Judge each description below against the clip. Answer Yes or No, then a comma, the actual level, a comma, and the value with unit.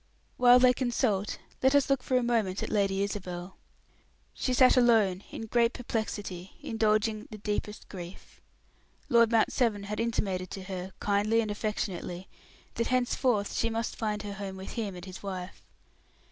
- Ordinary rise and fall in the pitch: Yes, average, 3.3 semitones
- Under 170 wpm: Yes, average, 160 wpm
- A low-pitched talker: No, high, 210 Hz